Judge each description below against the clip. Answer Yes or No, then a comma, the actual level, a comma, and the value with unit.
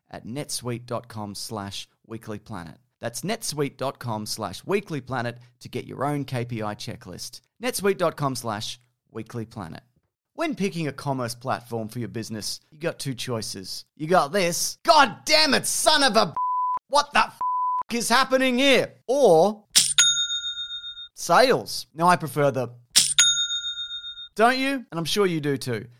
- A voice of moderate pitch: Yes, medium, 150 Hz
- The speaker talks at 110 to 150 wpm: Yes, slow, 135 wpm